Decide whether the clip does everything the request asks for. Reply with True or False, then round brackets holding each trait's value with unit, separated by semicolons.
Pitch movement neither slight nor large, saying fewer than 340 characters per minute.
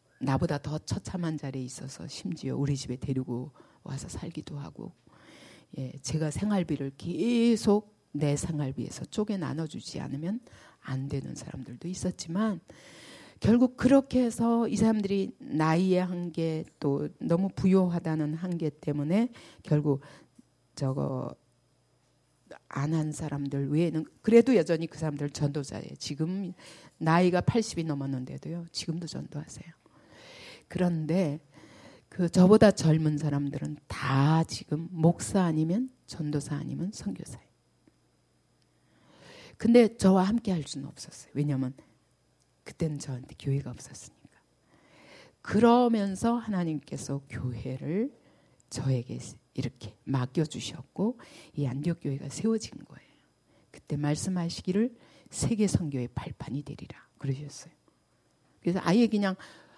True (4.9 semitones; 275 characters per minute)